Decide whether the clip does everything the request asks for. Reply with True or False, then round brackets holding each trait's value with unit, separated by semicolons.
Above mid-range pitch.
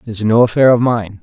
False (115 Hz)